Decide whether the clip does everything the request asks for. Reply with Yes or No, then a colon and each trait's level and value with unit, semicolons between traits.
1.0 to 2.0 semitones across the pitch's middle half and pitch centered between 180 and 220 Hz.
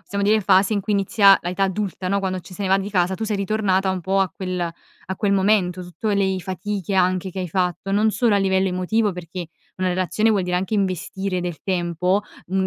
Yes: narrow, 1.6 semitones; high, 190 Hz